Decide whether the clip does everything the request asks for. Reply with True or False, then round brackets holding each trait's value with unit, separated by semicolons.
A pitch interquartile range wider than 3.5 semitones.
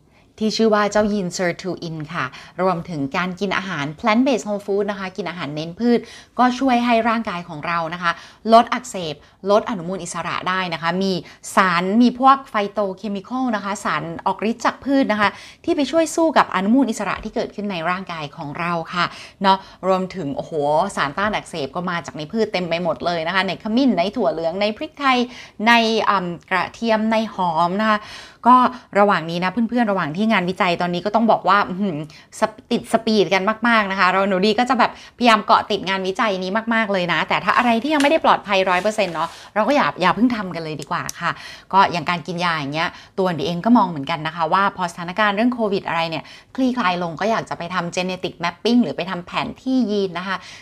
True (4.3 semitones)